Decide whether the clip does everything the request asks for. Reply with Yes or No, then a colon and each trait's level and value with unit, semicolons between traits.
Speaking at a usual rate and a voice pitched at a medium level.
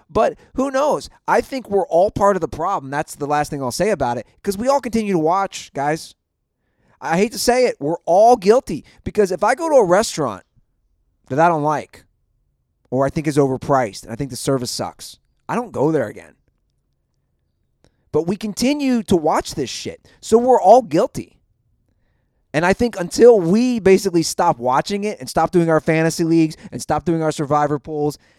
Yes: average, 195 wpm; medium, 165 Hz